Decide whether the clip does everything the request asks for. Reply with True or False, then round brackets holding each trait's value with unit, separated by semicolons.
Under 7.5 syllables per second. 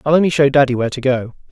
False (7.8 syllables/s)